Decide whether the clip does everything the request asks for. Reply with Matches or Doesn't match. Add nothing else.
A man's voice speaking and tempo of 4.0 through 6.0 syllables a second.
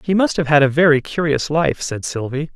Matches